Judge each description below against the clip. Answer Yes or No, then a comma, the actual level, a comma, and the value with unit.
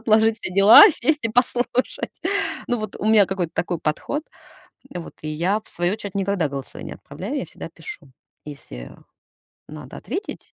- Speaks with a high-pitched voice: Yes, high, 200 Hz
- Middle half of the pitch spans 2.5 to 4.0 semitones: No, wide, 5.6 semitones